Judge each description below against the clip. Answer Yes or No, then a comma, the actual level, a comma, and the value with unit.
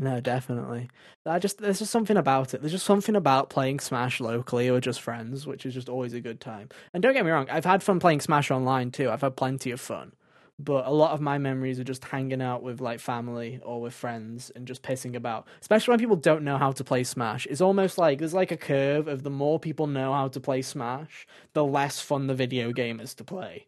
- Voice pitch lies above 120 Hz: Yes, low, 135 Hz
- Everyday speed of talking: No, fast, 245 wpm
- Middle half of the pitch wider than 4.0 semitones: No, average, 3.7 semitones